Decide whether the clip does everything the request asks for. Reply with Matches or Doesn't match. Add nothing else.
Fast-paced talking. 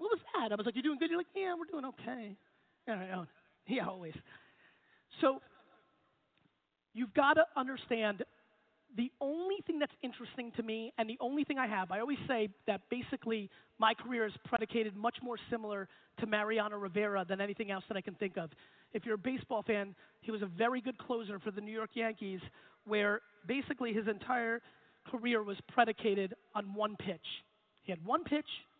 Doesn't match